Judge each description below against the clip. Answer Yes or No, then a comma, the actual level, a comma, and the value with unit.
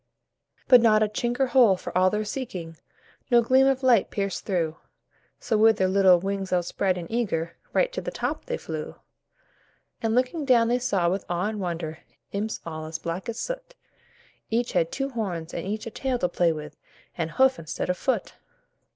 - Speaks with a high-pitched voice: Yes, high, 210 Hz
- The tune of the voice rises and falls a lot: Yes, wide, 5.7 semitones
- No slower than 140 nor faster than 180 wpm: No, average, 195 wpm